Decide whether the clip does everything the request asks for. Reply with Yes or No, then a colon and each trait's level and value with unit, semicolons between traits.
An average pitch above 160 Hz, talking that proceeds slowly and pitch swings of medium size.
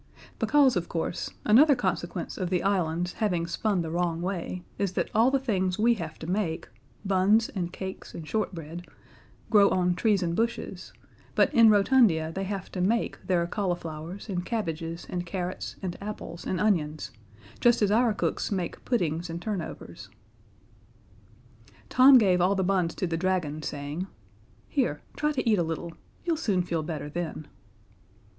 No: medium, 185 Hz; average, 165 wpm; average, 3.9 semitones